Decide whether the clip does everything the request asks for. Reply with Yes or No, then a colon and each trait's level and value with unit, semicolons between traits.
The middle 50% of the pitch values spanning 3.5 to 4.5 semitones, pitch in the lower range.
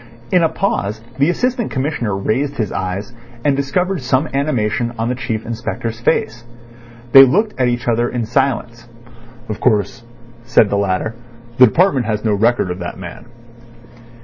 Yes: average, 4.2 semitones; low, 120 Hz